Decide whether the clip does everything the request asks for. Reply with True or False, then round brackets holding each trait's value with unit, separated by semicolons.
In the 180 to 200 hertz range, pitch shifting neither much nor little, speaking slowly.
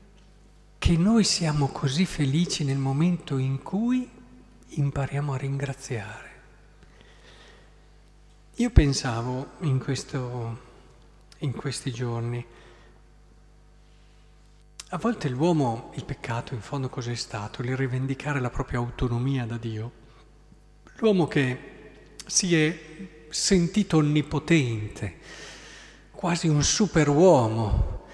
False (140 Hz; 4.5 semitones; 95 wpm)